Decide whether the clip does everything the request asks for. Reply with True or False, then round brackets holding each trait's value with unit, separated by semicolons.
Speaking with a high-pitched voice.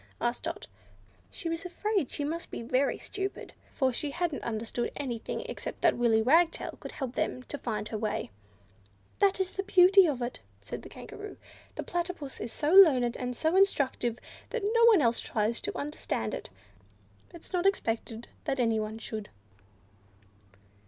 True (280 Hz)